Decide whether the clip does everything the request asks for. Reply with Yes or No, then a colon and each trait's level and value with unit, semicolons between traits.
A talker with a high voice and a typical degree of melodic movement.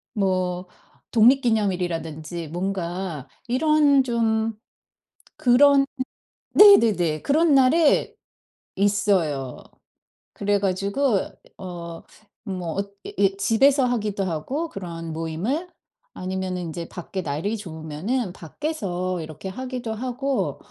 No: high, 195 Hz; wide, 6.2 semitones